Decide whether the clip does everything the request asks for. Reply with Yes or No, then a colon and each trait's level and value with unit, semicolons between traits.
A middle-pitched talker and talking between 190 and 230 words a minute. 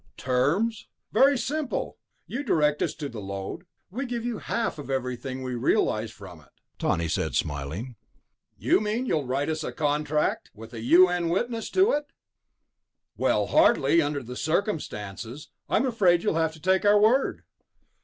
No: medium, 155 Hz; average, 160 wpm